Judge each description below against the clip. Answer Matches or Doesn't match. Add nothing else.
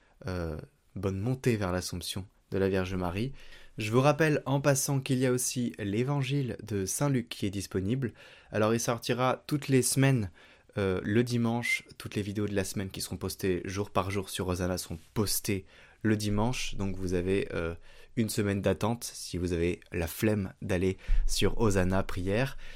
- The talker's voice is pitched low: Matches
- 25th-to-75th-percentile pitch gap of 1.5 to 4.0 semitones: Doesn't match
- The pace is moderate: Matches